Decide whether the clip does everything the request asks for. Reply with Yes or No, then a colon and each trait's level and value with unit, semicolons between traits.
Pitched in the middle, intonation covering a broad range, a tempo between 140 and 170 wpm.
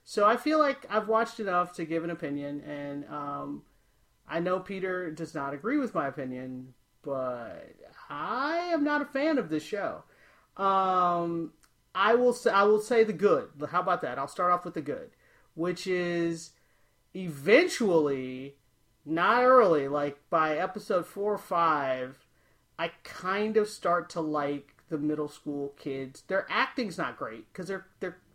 Yes: medium, 170 Hz; wide, 6.0 semitones; average, 165 wpm